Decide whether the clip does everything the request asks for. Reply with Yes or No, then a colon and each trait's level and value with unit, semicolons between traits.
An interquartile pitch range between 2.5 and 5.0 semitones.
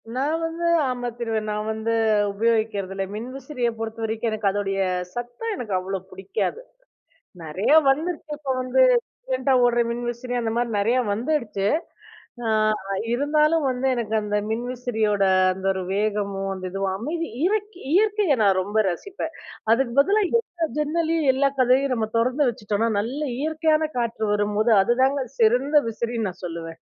No: wide, 5.5 semitones